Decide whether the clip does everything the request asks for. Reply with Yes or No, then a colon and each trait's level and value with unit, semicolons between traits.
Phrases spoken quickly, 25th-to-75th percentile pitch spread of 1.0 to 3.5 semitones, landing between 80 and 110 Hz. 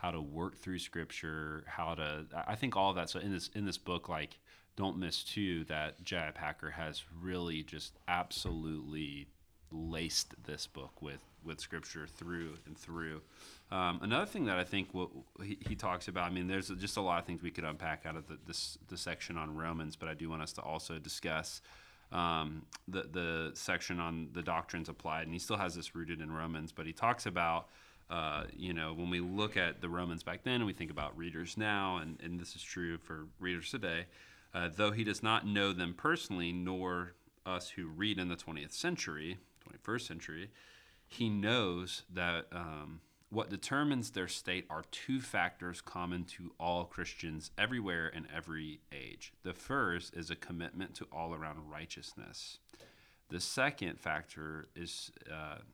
No: average, 185 wpm; narrow, 2.4 semitones; very low, 85 Hz